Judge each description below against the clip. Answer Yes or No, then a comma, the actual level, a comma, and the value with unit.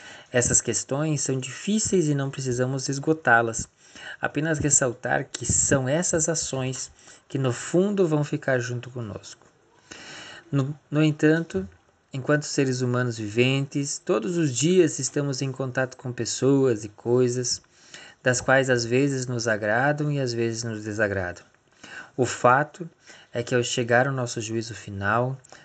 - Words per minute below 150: Yes, average, 140 wpm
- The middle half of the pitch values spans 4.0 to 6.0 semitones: No, average, 3.5 semitones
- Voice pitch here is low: Yes, low, 130 Hz